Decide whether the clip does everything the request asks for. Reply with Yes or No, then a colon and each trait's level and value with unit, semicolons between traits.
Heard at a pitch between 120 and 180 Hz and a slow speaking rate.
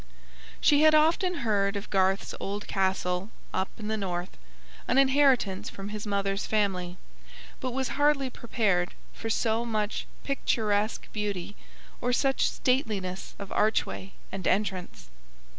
No: high, 210 Hz; slow, 130 wpm